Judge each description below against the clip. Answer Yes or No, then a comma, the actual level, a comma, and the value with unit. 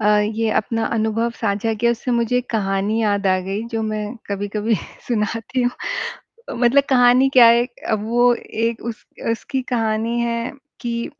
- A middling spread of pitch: No, narrow, 1.9 semitones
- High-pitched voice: Yes, high, 225 Hz